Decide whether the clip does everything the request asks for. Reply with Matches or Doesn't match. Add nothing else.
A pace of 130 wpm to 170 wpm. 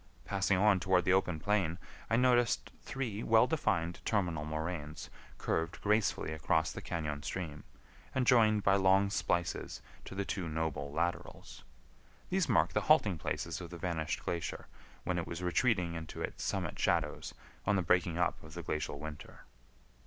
Matches